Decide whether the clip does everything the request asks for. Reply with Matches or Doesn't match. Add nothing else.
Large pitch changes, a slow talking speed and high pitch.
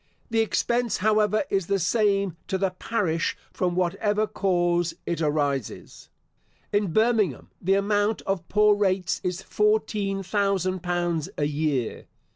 Doesn't match